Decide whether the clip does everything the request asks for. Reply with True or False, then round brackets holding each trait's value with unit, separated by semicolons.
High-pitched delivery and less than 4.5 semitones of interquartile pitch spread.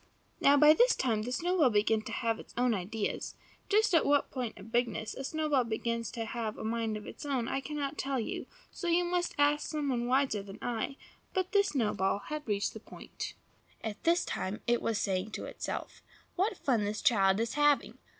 False (245 Hz; 5.2 semitones)